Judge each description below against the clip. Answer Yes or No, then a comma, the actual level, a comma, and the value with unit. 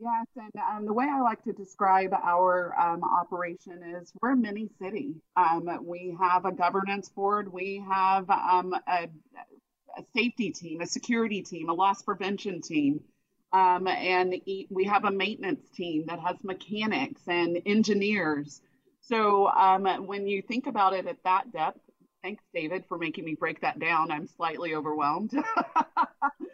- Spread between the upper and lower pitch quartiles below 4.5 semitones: Yes, average, 3.1 semitones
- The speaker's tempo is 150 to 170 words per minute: Yes, average, 160 wpm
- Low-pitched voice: No, high, 190 Hz